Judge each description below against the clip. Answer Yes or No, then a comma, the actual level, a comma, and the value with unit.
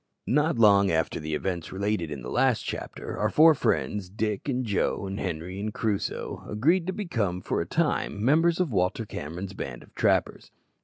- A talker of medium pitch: No, low, 100 Hz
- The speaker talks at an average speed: Yes, average, 185 wpm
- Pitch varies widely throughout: Yes, wide, 6.2 semitones